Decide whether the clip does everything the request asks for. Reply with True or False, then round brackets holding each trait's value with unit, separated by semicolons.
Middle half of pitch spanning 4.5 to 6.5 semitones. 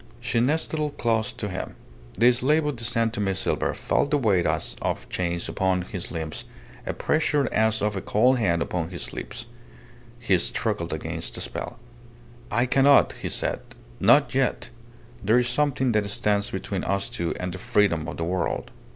True (5.0 semitones)